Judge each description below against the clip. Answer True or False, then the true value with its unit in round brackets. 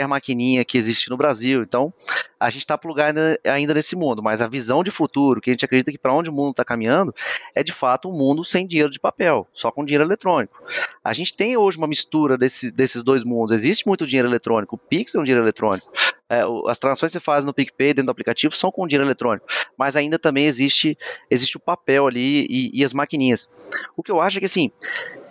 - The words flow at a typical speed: False (230 wpm)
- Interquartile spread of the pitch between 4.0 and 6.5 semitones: True (4.3 semitones)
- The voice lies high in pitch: False (140 Hz)